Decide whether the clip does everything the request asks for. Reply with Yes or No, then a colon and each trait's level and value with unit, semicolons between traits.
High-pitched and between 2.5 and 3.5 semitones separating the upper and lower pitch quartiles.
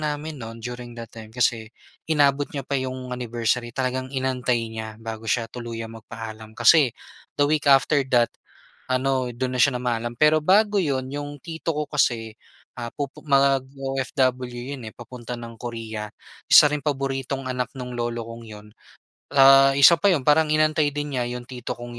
No: low, 130 Hz; average, 3.2 semitones